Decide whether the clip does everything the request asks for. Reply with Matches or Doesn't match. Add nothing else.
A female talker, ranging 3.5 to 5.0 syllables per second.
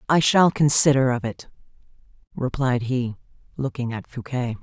Matches